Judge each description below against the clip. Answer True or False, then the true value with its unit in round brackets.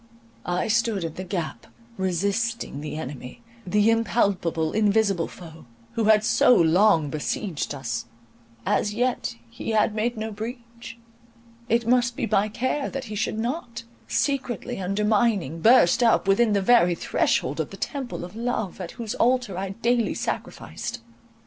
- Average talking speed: True (145 wpm)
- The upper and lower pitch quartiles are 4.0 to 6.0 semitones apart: True (5.2 semitones)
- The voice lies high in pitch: True (210 Hz)